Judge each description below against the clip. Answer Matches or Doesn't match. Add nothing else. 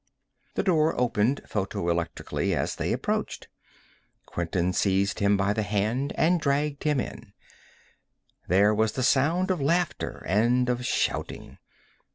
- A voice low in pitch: Matches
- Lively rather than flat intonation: Matches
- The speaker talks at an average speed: Doesn't match